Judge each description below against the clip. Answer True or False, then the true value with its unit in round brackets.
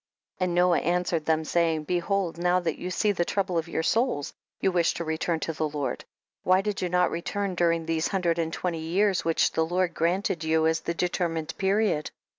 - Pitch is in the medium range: True (170 Hz)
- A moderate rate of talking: False (215 wpm)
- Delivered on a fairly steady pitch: True (2.1 semitones)